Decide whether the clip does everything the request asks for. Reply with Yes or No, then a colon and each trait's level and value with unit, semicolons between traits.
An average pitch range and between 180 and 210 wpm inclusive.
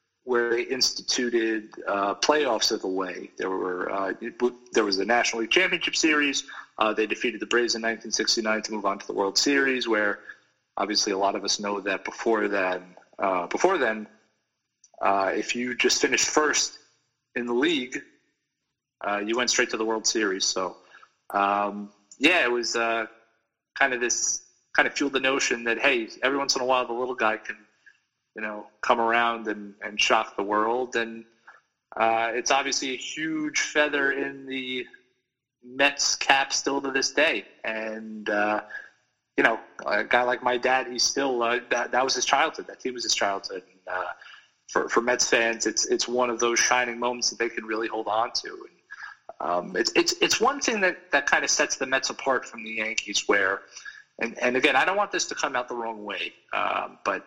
Yes: average, 3.0 semitones; average, 195 wpm